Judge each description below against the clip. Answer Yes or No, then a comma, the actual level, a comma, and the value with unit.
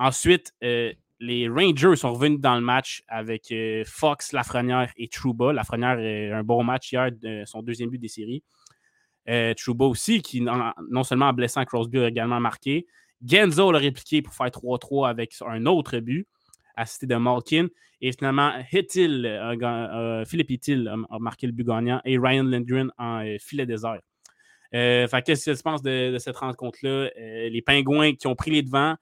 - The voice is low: Yes, low, 125 Hz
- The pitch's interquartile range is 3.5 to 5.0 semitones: No, average, 3.1 semitones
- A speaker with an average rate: Yes, average, 190 wpm